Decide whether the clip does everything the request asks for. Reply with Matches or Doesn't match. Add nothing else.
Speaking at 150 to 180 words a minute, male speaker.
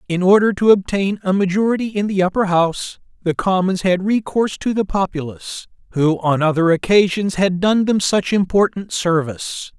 Matches